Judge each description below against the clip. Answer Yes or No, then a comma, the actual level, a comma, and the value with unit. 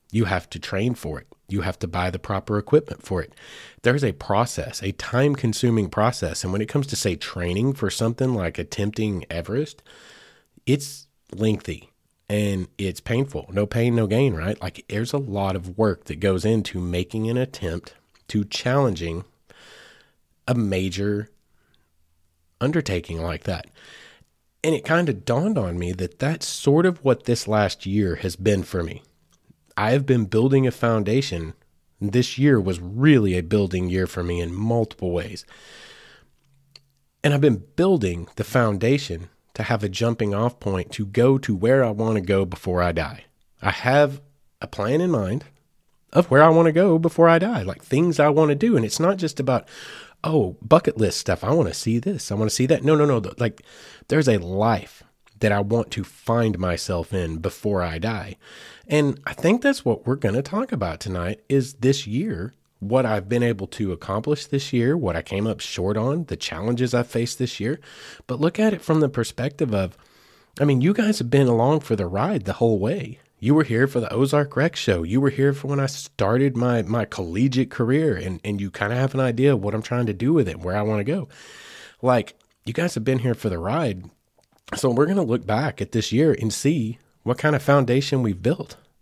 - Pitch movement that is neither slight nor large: No, wide, 6.0 semitones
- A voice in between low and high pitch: No, low, 115 Hz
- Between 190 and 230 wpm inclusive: Yes, average, 200 wpm